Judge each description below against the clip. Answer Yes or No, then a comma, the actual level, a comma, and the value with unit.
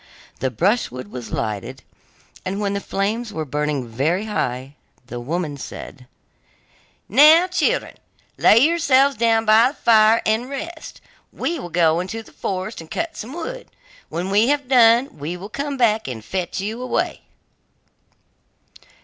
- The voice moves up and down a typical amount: No, wide, 8.1 semitones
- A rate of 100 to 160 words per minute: Yes, average, 150 wpm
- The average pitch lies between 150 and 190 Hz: No, high, 210 Hz